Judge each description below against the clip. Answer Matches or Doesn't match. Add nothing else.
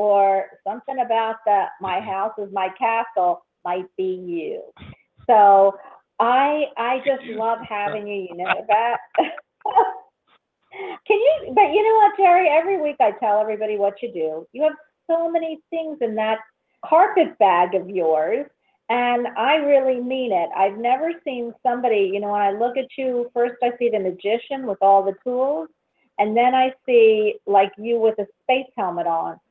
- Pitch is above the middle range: Matches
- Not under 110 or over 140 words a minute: Doesn't match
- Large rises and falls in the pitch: Matches